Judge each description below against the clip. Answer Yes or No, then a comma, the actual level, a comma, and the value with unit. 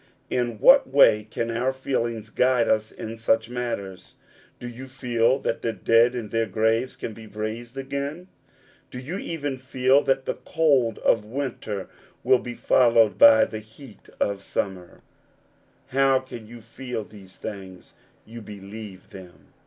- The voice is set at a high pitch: No, low, 115 Hz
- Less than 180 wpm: Yes, average, 155 wpm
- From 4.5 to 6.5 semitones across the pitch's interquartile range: No, average, 3.2 semitones